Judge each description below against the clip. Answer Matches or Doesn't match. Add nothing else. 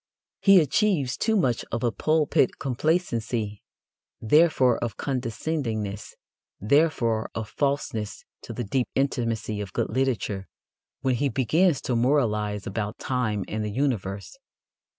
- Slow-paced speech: Matches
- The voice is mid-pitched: Doesn't match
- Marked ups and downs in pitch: Doesn't match